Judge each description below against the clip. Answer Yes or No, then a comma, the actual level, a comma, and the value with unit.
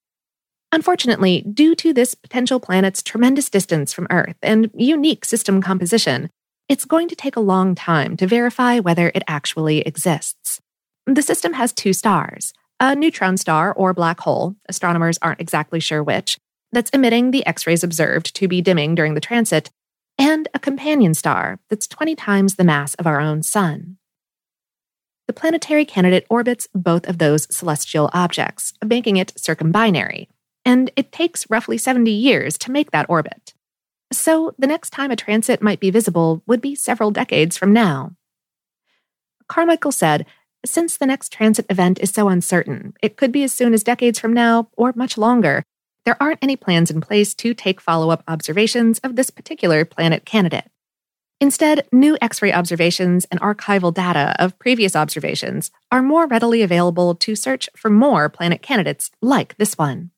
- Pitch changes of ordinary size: No, wide, 6.4 semitones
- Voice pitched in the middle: No, high, 205 Hz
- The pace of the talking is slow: No, average, 165 wpm